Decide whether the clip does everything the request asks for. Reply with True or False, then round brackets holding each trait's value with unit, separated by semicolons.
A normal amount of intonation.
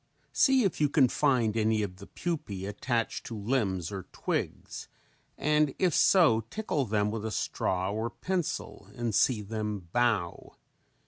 False (5.8 semitones)